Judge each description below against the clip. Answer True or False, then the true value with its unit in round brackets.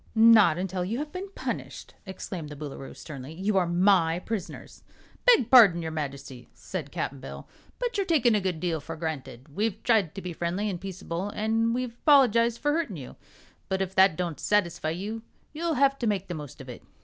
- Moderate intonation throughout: False (5.9 semitones)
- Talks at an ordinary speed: True (195 wpm)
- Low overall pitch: False (190 Hz)